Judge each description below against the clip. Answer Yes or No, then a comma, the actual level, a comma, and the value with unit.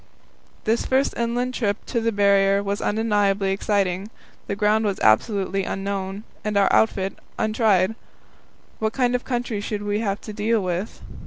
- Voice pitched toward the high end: Yes, high, 205 Hz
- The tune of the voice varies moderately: No, narrow, 2.2 semitones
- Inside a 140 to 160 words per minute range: Yes, average, 155 wpm